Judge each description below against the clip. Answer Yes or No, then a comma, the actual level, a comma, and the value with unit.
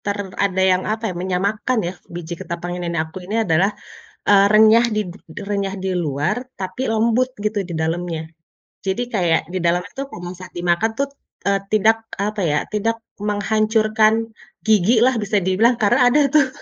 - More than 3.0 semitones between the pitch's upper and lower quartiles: Yes, average, 3.8 semitones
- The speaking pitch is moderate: No, high, 205 Hz